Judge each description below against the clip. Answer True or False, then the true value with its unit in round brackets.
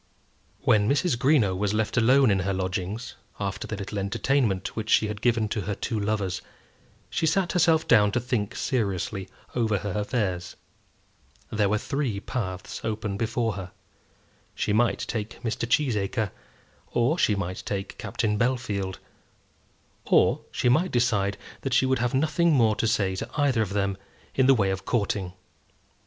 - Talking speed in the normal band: True (160 wpm)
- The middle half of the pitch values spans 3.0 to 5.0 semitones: True (3.9 semitones)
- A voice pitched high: False (110 Hz)